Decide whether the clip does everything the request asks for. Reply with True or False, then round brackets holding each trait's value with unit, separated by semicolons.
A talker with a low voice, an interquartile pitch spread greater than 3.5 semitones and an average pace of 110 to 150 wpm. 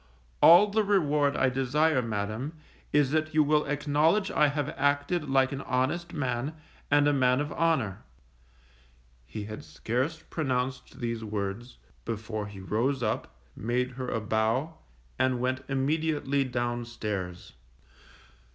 True (130 Hz; 4.1 semitones; 135 wpm)